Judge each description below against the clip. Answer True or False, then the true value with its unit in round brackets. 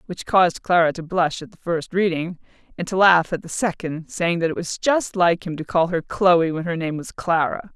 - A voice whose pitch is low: False (175 Hz)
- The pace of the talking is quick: True (240 wpm)